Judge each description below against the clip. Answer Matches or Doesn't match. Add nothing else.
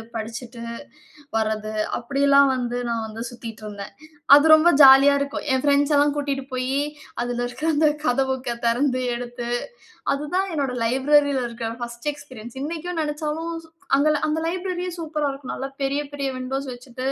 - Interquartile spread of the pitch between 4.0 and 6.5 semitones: Doesn't match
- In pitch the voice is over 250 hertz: Matches